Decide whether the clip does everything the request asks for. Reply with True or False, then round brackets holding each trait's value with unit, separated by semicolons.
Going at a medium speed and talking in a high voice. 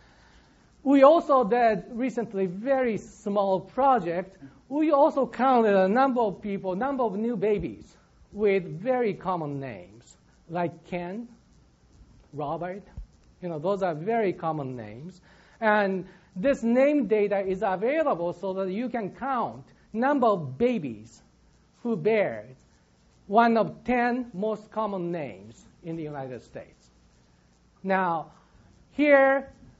False (120 wpm; 205 Hz)